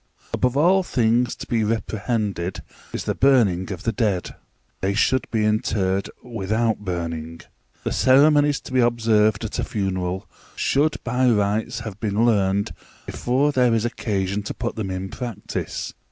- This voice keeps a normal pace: Yes, average, 155 wpm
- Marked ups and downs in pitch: No, average, 4.0 semitones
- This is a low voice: Yes, low, 110 Hz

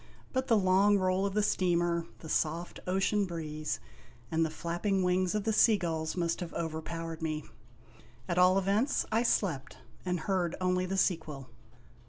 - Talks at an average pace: Yes, average, 165 wpm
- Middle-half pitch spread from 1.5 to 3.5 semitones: Yes, average, 2.9 semitones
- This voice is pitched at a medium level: Yes, medium, 180 Hz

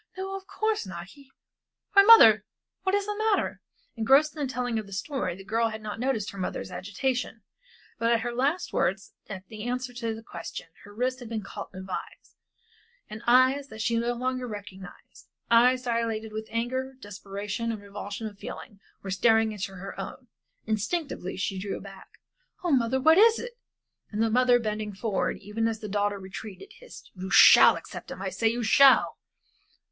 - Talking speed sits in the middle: Yes, average, 190 wpm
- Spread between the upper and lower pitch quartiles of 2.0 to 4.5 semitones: Yes, average, 4.1 semitones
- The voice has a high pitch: Yes, high, 225 Hz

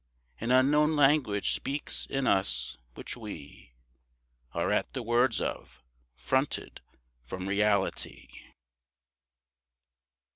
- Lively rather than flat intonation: Yes, wide, 5.7 semitones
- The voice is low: Yes, low, 120 Hz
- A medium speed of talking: No, slow, 95 wpm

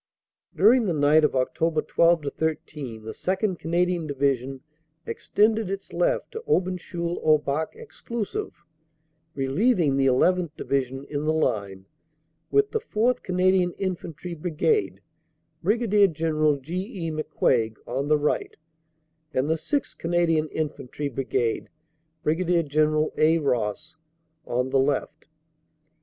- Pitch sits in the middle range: Yes, medium, 160 Hz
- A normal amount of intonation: Yes, average, 4.7 semitones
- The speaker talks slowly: Yes, slow, 125 wpm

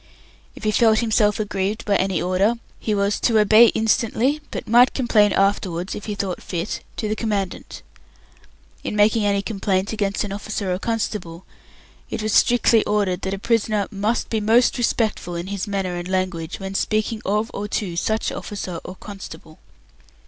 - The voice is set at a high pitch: Yes, high, 205 Hz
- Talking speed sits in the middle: Yes, average, 175 wpm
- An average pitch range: No, narrow, 2.3 semitones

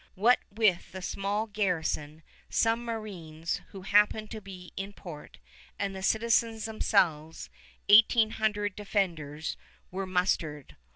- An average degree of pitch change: Yes, average, 3.8 semitones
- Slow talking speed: Yes, slow, 120 wpm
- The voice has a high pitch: Yes, high, 195 Hz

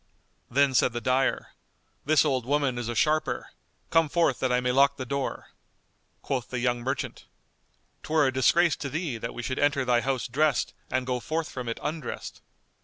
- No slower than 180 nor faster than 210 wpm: Yes, average, 185 wpm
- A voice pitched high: No, low, 130 Hz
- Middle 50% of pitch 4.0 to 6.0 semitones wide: No, average, 2.9 semitones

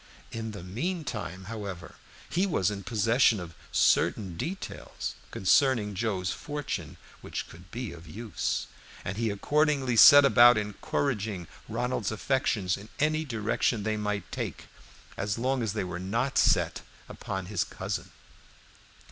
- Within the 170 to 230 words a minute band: No, average, 140 wpm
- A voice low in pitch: Yes, low, 110 Hz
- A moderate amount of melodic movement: Yes, average, 4.7 semitones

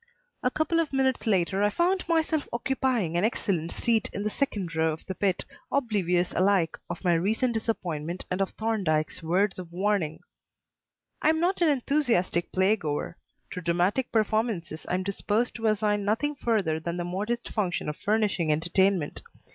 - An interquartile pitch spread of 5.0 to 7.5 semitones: Yes, average, 5.3 semitones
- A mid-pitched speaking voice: No, high, 200 Hz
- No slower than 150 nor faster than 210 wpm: Yes, average, 170 wpm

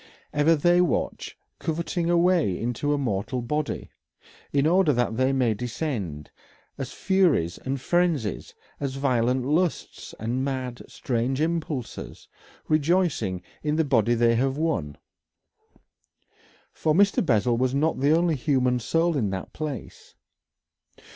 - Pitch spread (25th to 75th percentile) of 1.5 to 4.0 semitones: No, average, 5.0 semitones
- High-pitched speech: No, low, 135 Hz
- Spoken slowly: Yes, slow, 130 wpm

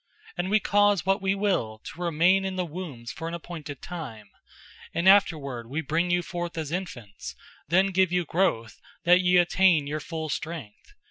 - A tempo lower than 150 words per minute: No, average, 180 wpm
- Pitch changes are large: No, average, 3.6 semitones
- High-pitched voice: No, medium, 170 Hz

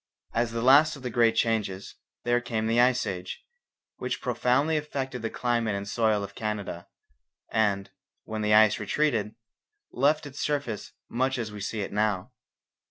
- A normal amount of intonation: Yes, average, 3.2 semitones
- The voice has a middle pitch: No, low, 115 Hz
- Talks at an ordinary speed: Yes, average, 165 wpm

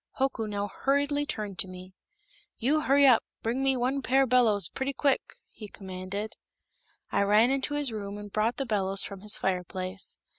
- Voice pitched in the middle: No, high, 220 Hz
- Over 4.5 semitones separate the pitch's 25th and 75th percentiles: Yes, average, 5.1 semitones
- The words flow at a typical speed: Yes, average, 175 wpm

